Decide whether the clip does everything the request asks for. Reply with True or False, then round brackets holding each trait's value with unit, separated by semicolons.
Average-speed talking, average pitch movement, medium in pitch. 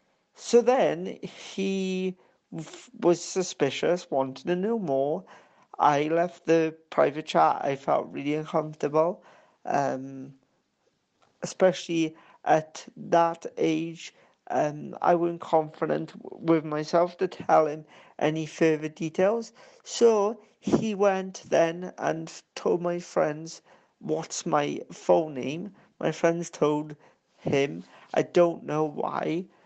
False (115 wpm; 3.1 semitones; 165 Hz)